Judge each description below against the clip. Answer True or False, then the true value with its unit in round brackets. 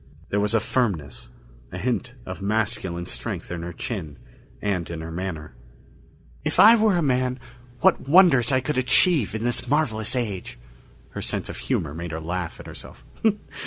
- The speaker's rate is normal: True (170 wpm)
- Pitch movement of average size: False (7.0 semitones)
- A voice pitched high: False (105 Hz)